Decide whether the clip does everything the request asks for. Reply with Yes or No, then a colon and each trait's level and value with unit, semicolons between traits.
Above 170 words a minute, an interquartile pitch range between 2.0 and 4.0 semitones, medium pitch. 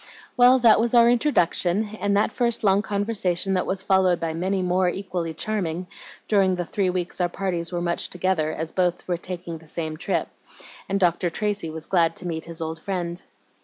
Yes: average, 190 wpm; average, 2.8 semitones; medium, 180 Hz